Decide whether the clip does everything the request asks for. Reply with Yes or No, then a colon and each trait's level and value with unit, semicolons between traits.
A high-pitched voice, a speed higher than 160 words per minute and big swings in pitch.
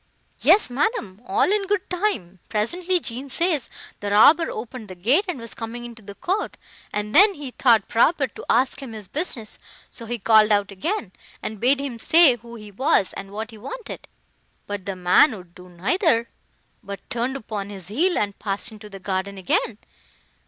Yes: high, 230 Hz; average, 185 wpm; wide, 6.5 semitones